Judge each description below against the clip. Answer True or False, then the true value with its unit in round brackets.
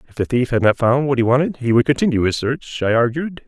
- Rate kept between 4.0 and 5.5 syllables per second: False (6.1 syllables/s)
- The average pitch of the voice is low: True (130 Hz)